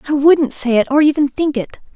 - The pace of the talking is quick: Yes, fast, 245 wpm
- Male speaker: No, female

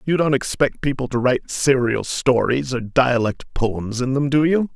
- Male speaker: Yes, male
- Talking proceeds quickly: No, average, 190 wpm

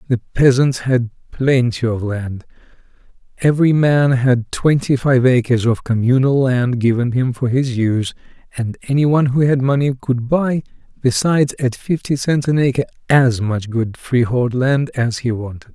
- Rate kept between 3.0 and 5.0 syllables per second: Yes, 4.7 syllables/s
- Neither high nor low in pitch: No, low, 125 Hz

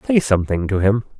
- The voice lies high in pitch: No, low, 110 Hz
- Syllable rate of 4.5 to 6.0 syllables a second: No, 6.4 syllables/s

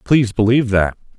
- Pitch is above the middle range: No, low, 115 Hz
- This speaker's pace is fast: No, average, 150 wpm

